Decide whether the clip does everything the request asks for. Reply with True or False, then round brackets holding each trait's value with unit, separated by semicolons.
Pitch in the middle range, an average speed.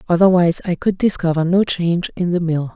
True (175 Hz; 195 wpm)